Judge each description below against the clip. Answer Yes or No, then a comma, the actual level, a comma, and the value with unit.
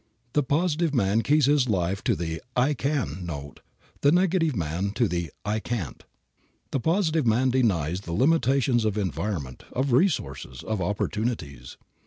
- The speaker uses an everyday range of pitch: No, wide, 8.5 semitones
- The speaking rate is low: No, average, 150 wpm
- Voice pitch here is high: No, low, 110 Hz